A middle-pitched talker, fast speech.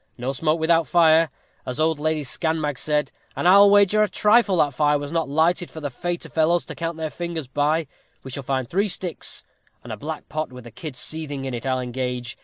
Yes: medium, 155 Hz; fast, 215 wpm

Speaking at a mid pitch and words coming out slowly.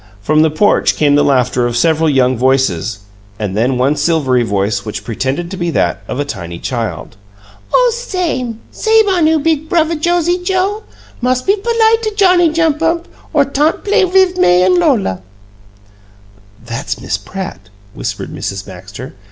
No: medium, 180 Hz; average, 165 wpm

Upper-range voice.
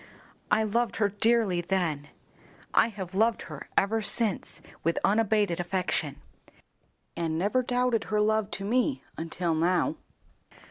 Yes: high, 205 Hz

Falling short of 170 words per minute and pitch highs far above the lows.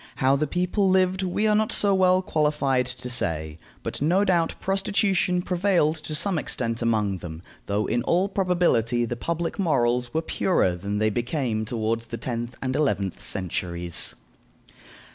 Yes: average, 160 wpm; wide, 7.9 semitones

